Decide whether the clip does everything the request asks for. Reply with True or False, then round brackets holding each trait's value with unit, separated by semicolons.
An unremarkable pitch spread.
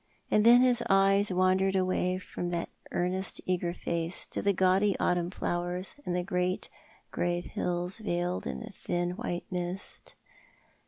False (1.6 semitones)